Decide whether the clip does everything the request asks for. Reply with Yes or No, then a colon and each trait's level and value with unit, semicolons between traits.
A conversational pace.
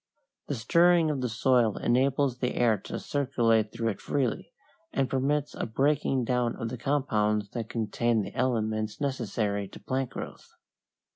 Yes: average, 155 wpm